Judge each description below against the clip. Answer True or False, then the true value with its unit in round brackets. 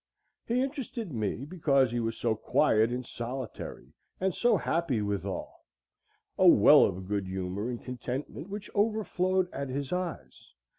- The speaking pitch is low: True (130 Hz)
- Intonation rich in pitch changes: True (8.5 semitones)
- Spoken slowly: False (145 wpm)